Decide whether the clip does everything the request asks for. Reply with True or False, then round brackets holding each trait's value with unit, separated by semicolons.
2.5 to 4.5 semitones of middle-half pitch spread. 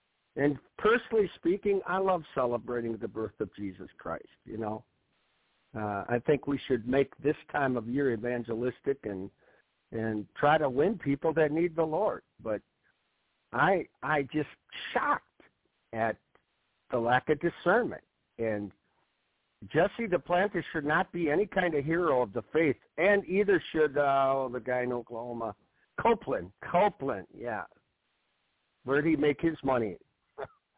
False (5.6 semitones)